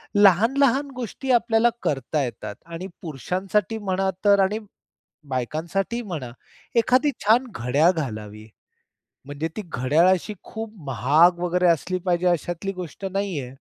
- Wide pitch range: Yes, wide, 5.8 semitones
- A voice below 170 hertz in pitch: No, medium, 180 Hz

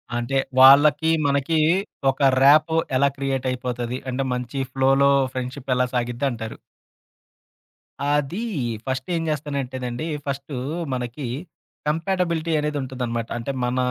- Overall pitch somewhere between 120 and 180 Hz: Yes, low, 135 Hz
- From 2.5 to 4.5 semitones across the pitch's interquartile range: Yes, average, 2.8 semitones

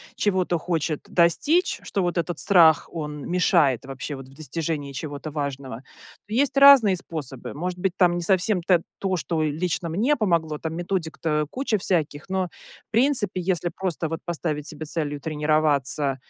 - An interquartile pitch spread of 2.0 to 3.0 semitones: No, average, 3.7 semitones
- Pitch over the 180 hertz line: No, medium, 165 Hz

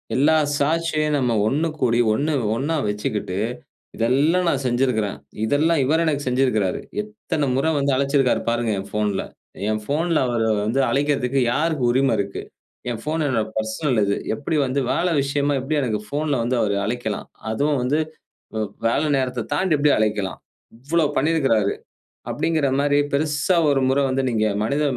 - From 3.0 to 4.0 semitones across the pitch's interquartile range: No, average, 4.7 semitones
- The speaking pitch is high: No, low, 135 Hz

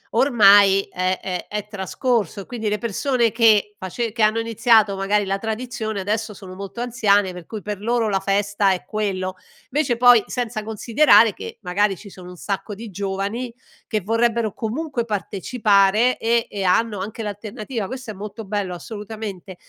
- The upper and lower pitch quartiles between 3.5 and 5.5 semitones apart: No, average, 2.7 semitones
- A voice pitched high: Yes, high, 210 Hz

